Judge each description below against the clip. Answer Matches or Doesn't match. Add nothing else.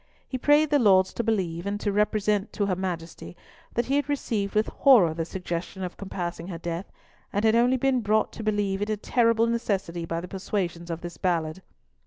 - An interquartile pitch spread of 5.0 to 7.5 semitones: Doesn't match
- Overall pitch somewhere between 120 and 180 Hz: Doesn't match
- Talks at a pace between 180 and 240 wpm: Matches